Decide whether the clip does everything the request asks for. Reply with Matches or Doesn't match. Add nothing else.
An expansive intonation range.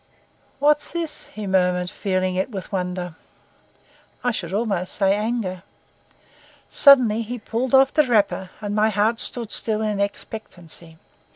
Doesn't match